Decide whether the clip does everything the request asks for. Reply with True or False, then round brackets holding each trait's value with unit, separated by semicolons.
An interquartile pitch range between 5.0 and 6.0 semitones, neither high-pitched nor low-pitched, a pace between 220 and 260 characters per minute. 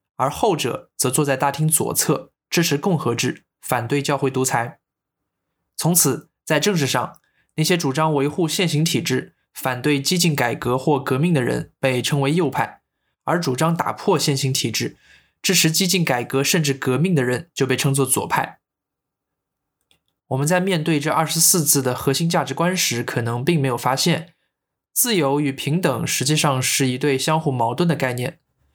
False (4.1 semitones; 145 Hz; 255 characters per minute)